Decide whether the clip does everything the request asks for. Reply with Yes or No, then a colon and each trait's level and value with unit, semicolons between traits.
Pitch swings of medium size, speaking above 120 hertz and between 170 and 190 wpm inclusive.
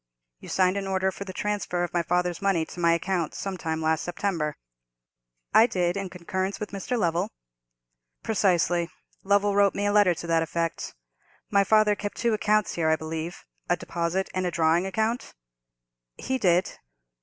Yes: average, 3.0 semitones; medium, 185 Hz; average, 175 wpm